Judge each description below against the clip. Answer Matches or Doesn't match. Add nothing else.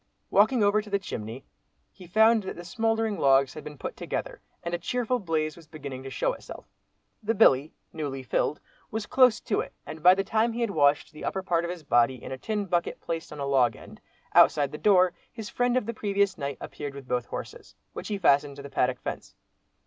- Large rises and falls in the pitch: Matches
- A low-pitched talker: Doesn't match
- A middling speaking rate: Doesn't match